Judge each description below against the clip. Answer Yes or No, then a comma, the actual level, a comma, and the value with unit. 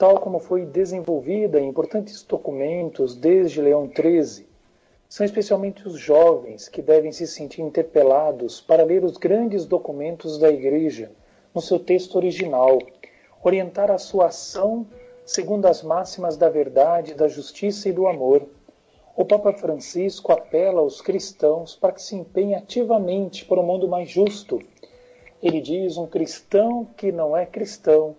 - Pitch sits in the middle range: Yes, medium, 180 Hz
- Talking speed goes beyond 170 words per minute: No, average, 145 wpm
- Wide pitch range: No, average, 4.2 semitones